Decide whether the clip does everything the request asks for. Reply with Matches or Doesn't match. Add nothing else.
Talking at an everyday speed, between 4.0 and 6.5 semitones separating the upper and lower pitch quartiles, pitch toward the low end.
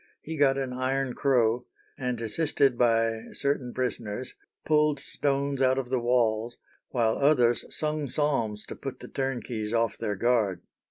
Doesn't match